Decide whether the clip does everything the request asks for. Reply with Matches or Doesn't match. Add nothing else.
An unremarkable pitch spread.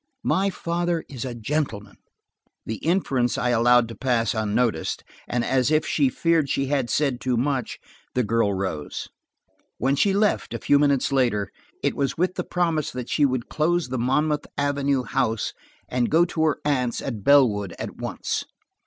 Matches